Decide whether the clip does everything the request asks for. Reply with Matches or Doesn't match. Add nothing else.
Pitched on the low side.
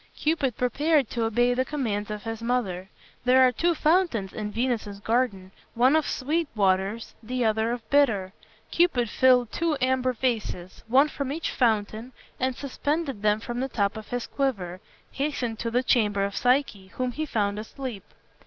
Doesn't match